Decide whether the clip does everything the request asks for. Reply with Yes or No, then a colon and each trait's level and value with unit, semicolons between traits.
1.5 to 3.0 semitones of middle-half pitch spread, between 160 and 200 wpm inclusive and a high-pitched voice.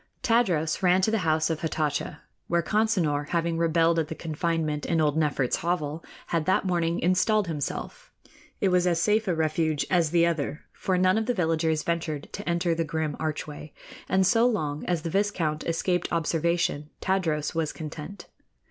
No: narrow, 2.6 semitones; average, 175 wpm; medium, 165 Hz